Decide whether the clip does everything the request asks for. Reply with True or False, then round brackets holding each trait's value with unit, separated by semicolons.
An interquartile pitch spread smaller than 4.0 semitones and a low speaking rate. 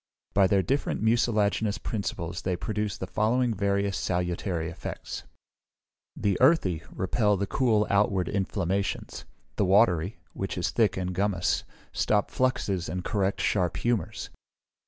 True (2.6 semitones; 130 wpm)